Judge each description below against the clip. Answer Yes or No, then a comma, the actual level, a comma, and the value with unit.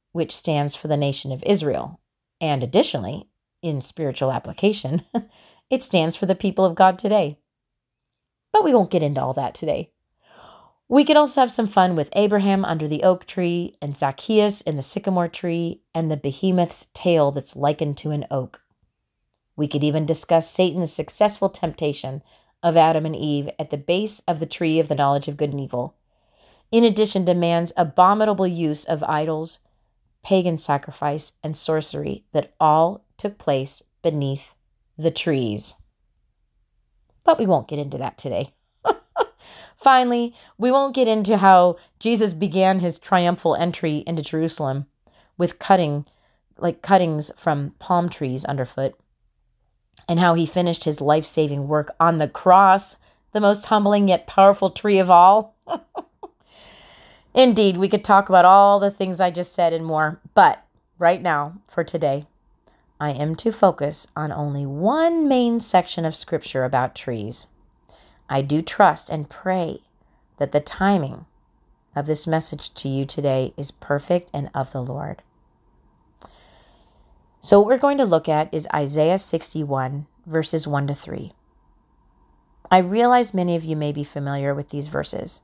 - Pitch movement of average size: Yes, average, 4.7 semitones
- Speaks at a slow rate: No, average, 155 wpm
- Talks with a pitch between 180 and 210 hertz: No, medium, 165 Hz